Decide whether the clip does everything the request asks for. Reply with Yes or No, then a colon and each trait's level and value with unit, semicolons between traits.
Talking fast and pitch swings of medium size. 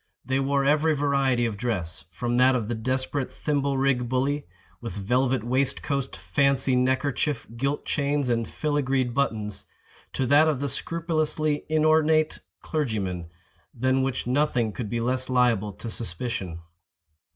No: average, 140 wpm; average, 3.3 semitones